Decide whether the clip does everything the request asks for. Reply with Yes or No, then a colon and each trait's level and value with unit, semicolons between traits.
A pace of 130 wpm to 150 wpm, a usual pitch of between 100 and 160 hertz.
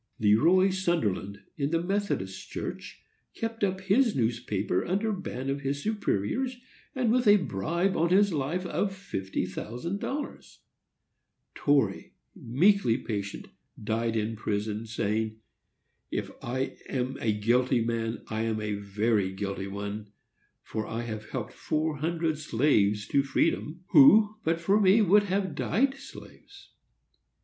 Yes: average, 140 wpm; low, 135 Hz